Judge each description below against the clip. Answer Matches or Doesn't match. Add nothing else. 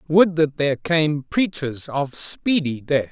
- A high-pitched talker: Doesn't match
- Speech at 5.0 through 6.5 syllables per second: Doesn't match